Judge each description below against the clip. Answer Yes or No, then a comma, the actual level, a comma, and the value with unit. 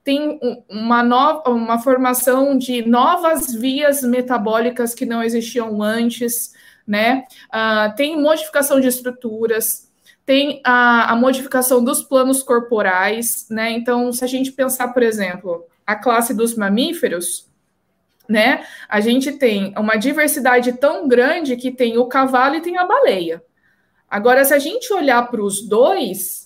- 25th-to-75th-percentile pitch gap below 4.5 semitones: Yes, average, 2.8 semitones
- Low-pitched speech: No, high, 245 Hz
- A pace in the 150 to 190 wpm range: No, average, 140 wpm